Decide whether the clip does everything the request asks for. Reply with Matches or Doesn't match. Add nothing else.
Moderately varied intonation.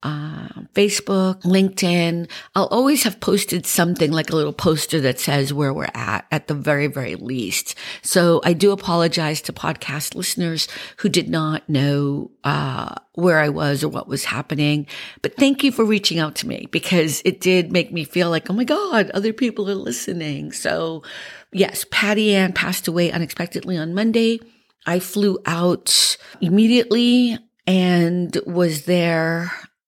Matches